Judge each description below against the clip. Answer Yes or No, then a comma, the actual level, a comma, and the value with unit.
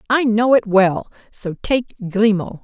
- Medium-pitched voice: No, high, 210 Hz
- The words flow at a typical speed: Yes, average, 160 wpm